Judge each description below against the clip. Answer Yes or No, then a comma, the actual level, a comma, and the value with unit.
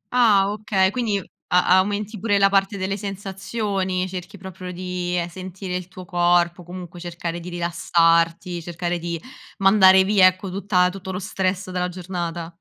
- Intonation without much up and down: Yes, narrow, 1.9 semitones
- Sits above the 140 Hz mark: Yes, medium, 185 Hz